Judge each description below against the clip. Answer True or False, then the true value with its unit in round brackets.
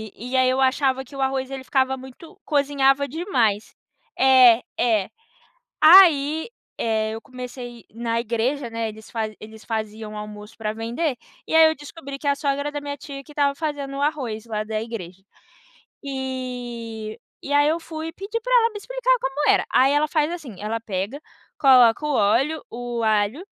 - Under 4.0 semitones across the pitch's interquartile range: False (4.3 semitones)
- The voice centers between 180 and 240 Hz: False (260 Hz)